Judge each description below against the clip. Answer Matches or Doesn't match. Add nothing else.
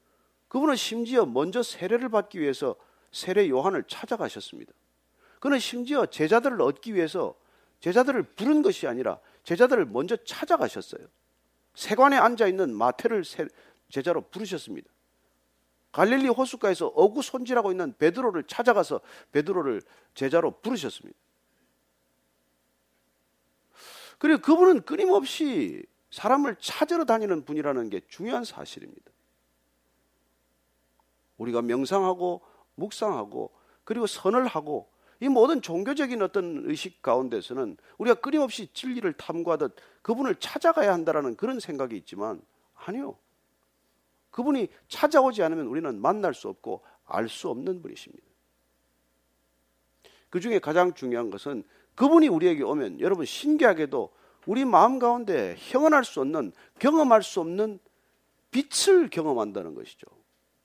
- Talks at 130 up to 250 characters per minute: Doesn't match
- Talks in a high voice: Matches